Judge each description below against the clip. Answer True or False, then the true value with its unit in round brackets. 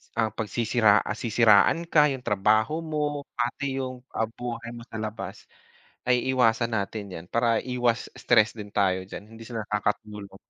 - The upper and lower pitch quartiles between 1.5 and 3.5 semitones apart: True (2.8 semitones)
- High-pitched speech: False (115 Hz)